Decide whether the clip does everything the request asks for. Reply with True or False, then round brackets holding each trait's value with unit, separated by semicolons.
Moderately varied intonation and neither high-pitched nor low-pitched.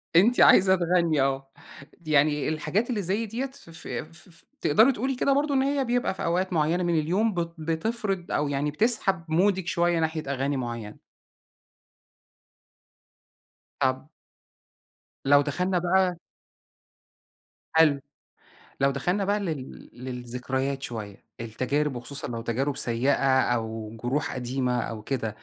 False (6.0 semitones; 155 Hz)